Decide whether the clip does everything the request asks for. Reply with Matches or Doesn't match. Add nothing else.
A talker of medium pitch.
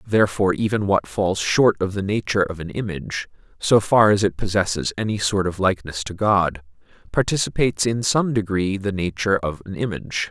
Doesn't match